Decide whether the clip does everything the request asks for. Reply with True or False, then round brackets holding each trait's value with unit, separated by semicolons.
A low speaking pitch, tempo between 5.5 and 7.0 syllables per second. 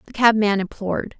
False (210 Hz; 5.7 syllables/s)